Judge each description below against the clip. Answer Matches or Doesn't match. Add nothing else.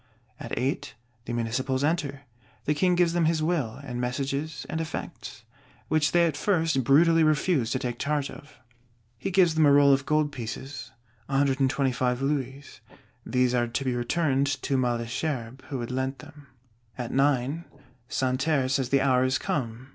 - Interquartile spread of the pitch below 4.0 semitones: Matches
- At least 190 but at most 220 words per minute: Doesn't match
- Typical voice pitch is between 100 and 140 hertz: Matches